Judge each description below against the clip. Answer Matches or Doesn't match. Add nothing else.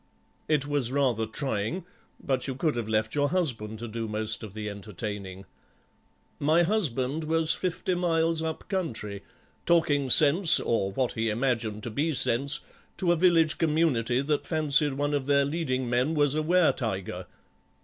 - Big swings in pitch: Matches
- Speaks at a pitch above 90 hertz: Matches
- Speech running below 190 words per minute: Matches